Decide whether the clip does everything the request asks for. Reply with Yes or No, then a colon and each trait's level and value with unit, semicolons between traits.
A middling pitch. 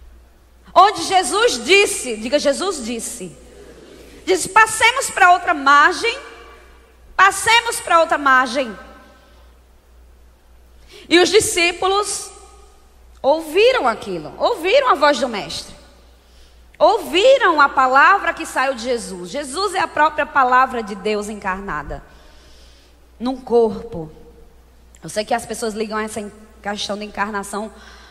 No: very high, 260 Hz